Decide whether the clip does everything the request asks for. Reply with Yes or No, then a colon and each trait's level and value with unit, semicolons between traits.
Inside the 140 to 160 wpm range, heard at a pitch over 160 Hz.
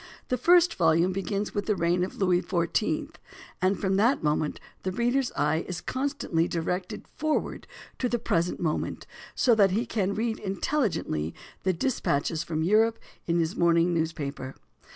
Yes: average, 155 wpm; medium, 185 Hz